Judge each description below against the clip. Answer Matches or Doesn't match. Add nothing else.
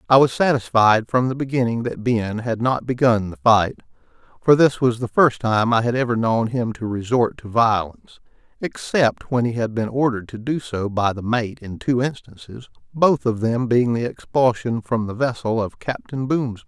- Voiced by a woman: Doesn't match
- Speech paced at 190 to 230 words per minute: Matches